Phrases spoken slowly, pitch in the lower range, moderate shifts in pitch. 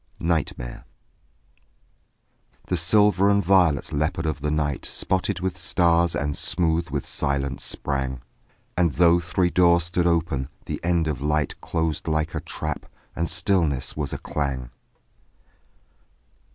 Yes: slow, 130 wpm; very low, 80 Hz; average, 3.2 semitones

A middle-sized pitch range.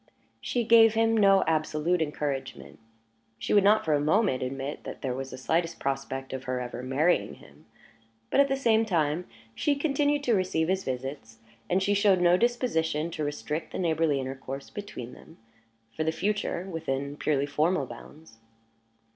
No: wide, 6.8 semitones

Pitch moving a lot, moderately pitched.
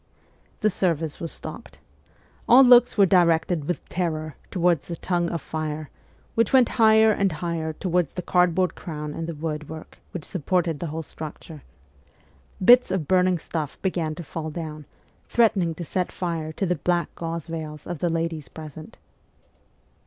No: narrow, 2.6 semitones; medium, 170 Hz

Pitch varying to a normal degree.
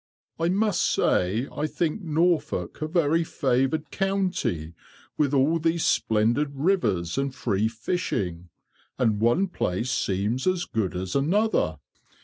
No: wide, 7.9 semitones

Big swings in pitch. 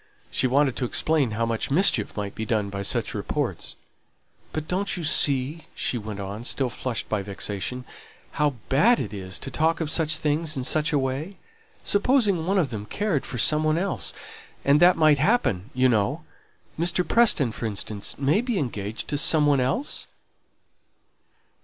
Yes: wide, 6.3 semitones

